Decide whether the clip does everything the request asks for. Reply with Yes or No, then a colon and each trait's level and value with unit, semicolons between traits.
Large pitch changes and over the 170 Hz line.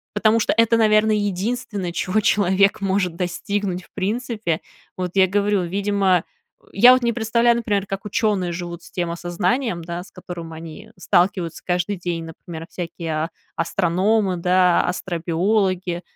No: average, 3.1 semitones; high, 190 Hz